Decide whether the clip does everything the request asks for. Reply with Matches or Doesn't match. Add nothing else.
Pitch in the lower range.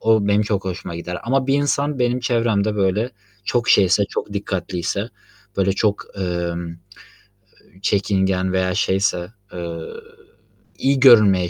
Matches